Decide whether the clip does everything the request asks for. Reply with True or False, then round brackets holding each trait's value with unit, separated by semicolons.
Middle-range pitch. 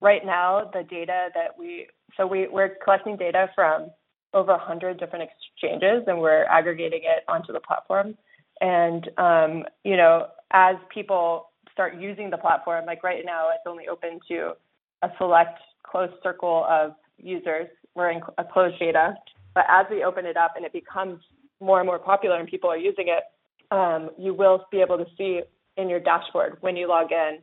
True (180 Hz)